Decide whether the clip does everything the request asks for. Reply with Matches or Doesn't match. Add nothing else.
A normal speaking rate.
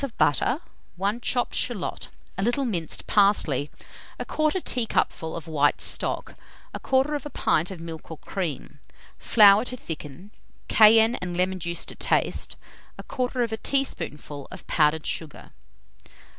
Doesn't match